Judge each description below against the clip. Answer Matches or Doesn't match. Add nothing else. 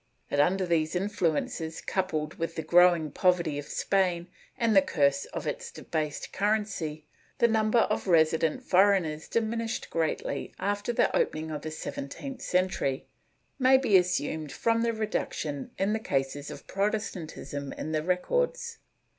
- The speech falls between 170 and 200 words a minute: Doesn't match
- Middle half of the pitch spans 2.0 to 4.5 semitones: Doesn't match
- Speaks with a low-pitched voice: Doesn't match